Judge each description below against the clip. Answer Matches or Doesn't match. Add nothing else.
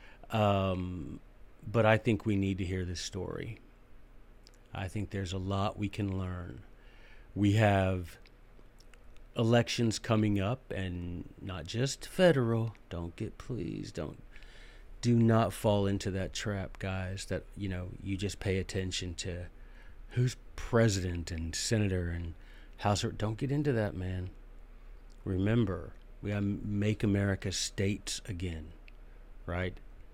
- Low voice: Matches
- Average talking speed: Doesn't match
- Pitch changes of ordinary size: Matches